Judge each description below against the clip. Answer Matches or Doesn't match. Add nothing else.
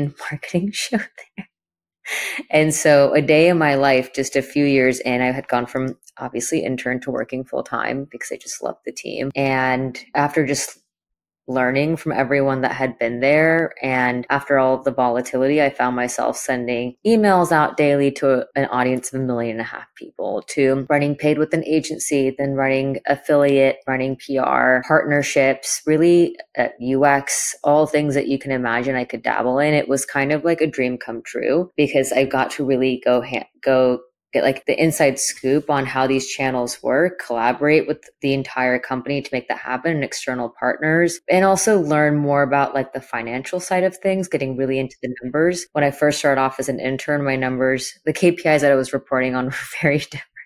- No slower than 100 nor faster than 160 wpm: Doesn't match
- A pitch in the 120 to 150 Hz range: Matches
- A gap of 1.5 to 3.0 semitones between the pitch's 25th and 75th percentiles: Matches